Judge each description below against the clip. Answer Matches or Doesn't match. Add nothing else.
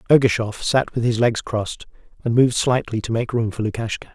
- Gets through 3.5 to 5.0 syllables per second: Doesn't match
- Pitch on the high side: Doesn't match